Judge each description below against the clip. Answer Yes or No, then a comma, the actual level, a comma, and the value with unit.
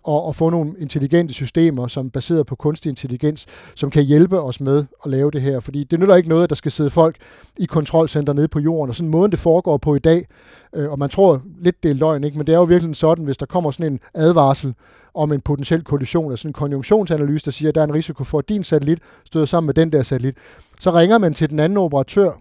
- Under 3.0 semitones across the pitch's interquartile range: Yes, narrow, 2.6 semitones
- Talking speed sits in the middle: No, fast, 255 wpm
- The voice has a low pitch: No, medium, 155 Hz